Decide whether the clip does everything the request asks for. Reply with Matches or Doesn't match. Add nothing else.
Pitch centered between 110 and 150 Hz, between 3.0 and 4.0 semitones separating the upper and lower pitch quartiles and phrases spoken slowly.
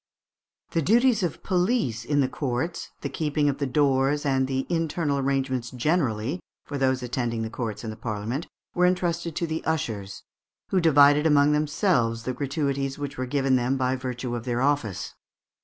Doesn't match